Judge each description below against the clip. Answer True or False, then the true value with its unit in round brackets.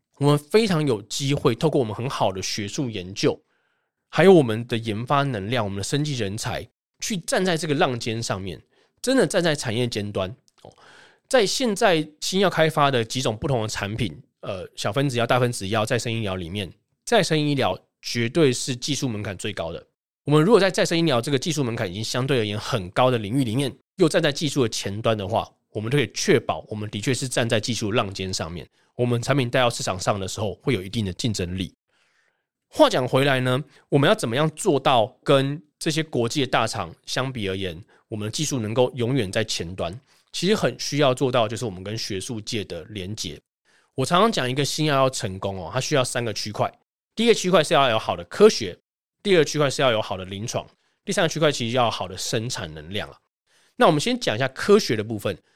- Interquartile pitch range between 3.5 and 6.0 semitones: True (5.2 semitones)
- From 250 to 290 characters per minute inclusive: False (325 characters per minute)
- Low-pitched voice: True (125 Hz)